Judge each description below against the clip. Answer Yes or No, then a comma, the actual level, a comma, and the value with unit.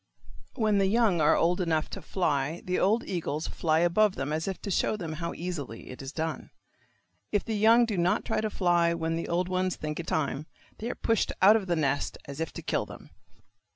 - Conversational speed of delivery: No, fast, 220 wpm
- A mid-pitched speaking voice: Yes, medium, 175 Hz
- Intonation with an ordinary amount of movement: Yes, average, 4.1 semitones